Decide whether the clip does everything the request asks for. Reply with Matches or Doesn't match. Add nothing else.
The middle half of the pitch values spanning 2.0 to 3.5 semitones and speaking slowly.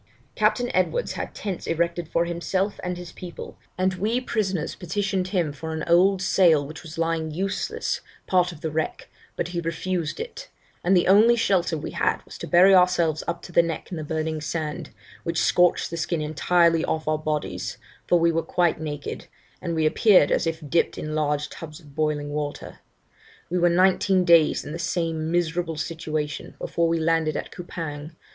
Doesn't match